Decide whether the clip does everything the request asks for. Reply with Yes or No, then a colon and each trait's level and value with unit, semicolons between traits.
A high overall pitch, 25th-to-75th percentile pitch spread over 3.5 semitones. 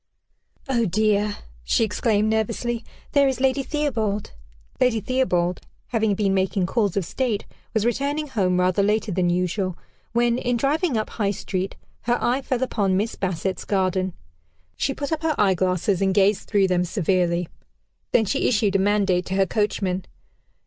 Yes: high, 205 Hz; average, 4.2 semitones